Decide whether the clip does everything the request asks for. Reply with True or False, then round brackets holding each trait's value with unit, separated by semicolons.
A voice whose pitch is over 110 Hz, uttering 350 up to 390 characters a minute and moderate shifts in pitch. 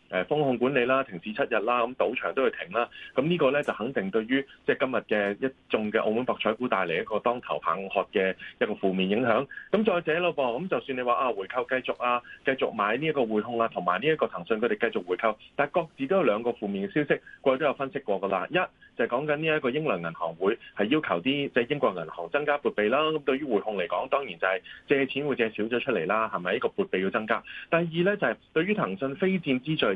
True (130 Hz; 375 characters per minute; 5.0 semitones)